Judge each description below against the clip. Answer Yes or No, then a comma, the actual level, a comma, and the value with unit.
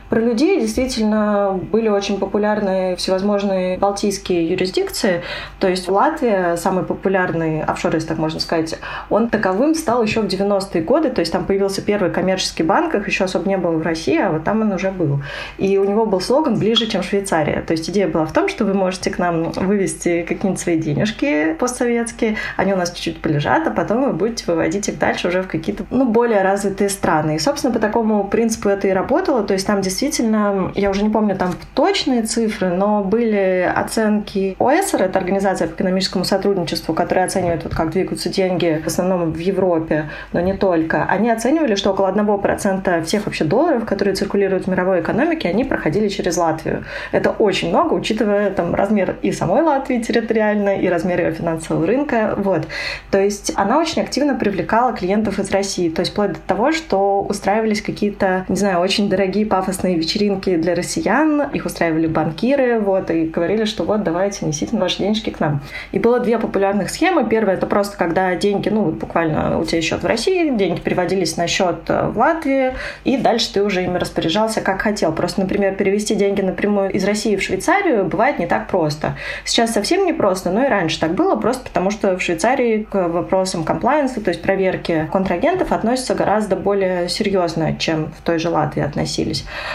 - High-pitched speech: Yes, high, 195 Hz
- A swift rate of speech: Yes, fast, 185 wpm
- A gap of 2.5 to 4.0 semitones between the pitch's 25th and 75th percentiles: Yes, average, 3.1 semitones